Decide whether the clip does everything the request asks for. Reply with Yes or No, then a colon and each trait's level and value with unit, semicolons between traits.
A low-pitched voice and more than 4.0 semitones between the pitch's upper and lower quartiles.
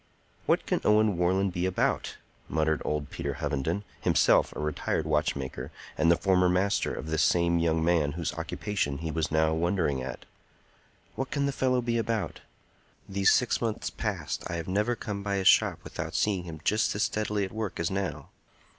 Yes: very low, 90 Hz; average, 4.5 semitones